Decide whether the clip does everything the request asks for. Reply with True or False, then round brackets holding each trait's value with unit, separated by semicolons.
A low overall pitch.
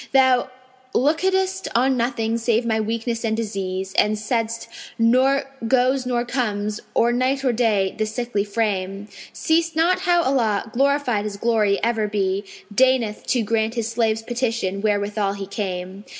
False (230 Hz)